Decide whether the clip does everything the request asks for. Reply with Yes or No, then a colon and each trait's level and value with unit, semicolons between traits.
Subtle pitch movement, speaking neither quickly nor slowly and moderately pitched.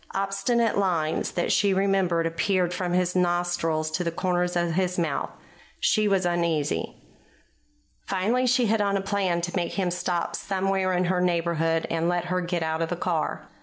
Yes: narrow, 2.3 semitones; average, 175 wpm; medium, 180 Hz